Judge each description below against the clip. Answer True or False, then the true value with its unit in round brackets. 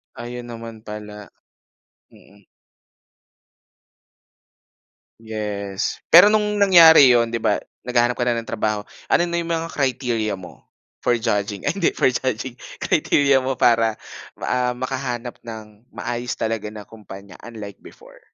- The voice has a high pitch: False (120 Hz)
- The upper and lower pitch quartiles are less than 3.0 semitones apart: False (3.4 semitones)